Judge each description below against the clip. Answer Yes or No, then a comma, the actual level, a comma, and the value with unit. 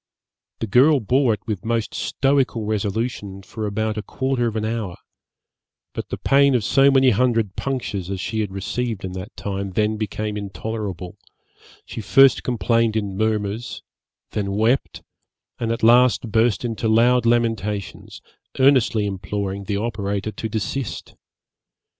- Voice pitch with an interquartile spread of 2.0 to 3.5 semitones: Yes, average, 3.0 semitones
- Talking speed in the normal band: Yes, average, 145 wpm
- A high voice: No, low, 110 Hz